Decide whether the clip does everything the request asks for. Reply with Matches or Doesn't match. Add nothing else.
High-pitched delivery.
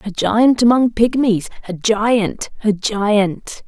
Matches